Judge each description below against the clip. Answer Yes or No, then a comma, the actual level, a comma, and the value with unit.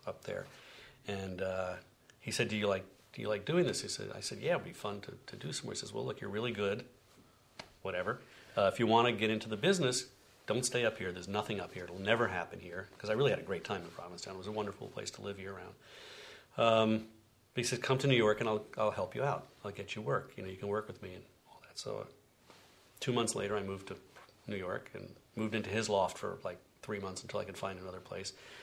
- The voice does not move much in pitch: No, average, 3.1 semitones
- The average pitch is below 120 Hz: Yes, low, 105 Hz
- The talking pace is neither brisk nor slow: No, fast, 260 wpm